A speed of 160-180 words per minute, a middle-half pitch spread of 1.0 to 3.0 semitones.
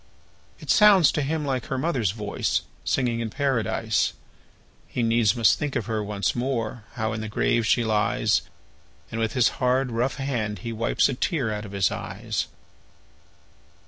No: average, 170 wpm; average, 3.6 semitones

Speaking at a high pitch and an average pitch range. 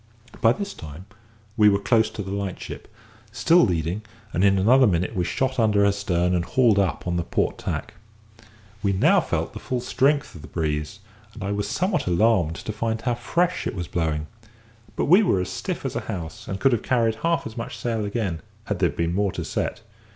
No: low, 100 Hz; average, 4.7 semitones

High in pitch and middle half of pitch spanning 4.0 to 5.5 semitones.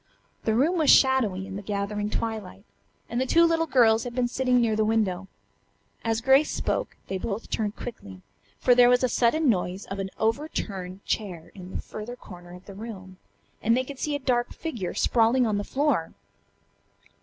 Yes: high, 225 Hz; average, 4.4 semitones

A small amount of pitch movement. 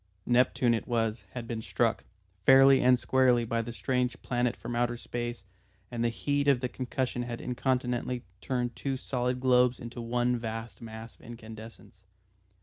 Yes: narrow, 1.4 semitones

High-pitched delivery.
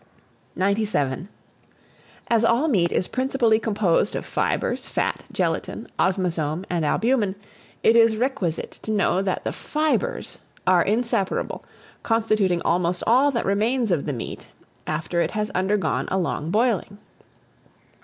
Yes: high, 200 Hz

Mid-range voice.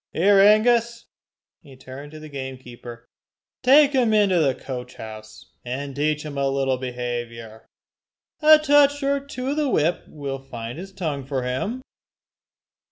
Yes: medium, 145 Hz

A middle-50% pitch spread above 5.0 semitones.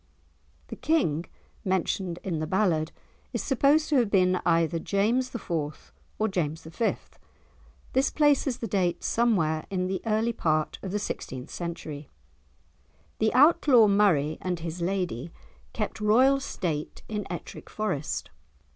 Yes: wide, 5.6 semitones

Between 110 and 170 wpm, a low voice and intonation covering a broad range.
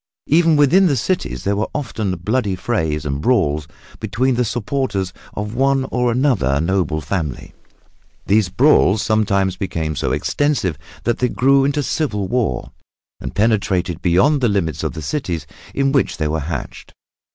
Yes: average, 155 wpm; low, 105 Hz; wide, 7.3 semitones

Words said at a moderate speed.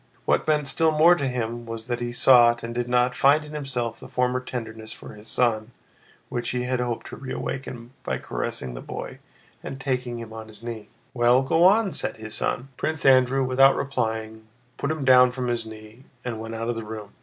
No: fast, 210 wpm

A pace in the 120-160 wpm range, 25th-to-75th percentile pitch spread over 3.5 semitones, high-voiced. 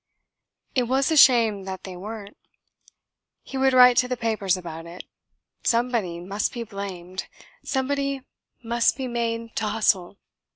Yes: average, 140 wpm; average, 4.6 semitones; high, 225 Hz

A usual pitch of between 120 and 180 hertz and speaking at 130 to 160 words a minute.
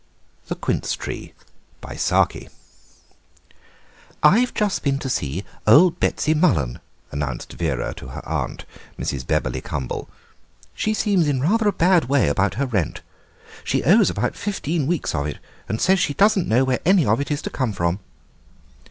Yes: medium, 140 Hz; average, 155 wpm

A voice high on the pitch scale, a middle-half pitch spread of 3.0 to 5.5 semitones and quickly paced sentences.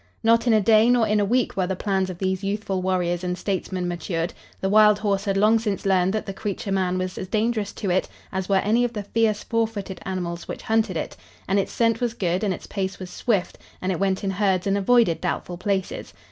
No: high, 195 Hz; narrow, 2.6 semitones; fast, 240 wpm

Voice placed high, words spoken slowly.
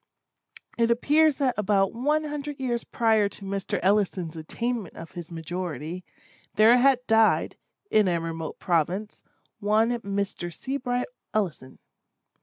Yes: high, 210 Hz; slow, 125 wpm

